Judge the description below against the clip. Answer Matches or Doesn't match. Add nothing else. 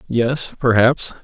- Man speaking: Matches